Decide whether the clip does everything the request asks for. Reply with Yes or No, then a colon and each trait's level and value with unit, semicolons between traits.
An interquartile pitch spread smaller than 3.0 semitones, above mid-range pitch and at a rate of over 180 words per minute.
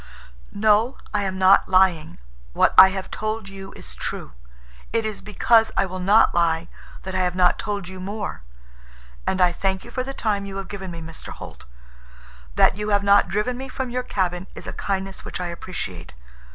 Yes: narrow, 2.4 semitones; high, 195 Hz; average, 195 wpm